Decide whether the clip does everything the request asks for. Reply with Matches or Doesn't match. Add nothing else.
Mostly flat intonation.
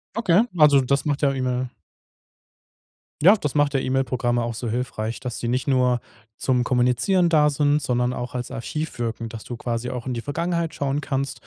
Doesn't match